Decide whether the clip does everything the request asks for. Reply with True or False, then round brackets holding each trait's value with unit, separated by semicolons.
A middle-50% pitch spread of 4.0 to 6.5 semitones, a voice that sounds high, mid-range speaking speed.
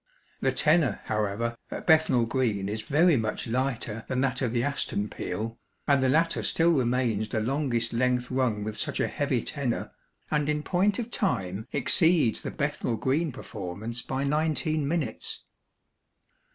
False (5.0 semitones; 130 Hz; 155 wpm)